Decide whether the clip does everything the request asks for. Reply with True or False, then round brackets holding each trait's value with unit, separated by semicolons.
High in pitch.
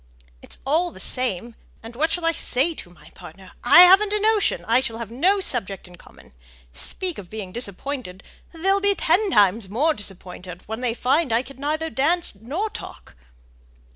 True (255 Hz)